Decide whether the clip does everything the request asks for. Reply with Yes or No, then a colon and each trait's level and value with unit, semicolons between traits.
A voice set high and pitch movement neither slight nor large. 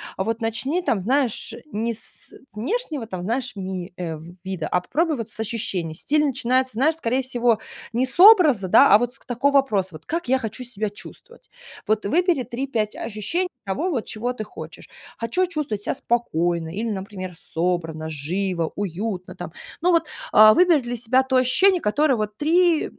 No: high, 230 Hz; wide, 5.9 semitones